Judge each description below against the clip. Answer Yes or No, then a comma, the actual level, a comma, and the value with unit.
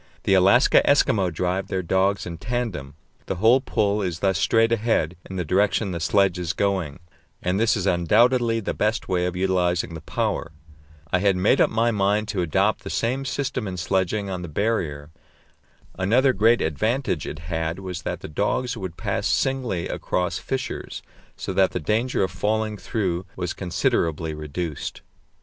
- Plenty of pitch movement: No, average, 3.8 semitones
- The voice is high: No, very low, 95 Hz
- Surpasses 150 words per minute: Yes, average, 170 wpm